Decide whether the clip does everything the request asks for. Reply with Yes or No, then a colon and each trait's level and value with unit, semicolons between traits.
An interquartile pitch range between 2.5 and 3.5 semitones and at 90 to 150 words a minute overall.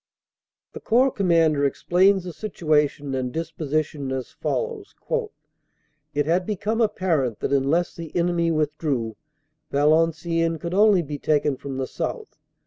No: average, 3.9 semitones; slow, 135 wpm